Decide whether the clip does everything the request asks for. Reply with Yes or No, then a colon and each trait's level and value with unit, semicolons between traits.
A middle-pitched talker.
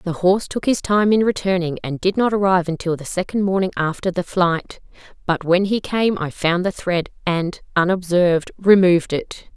Yes: medium, 180 Hz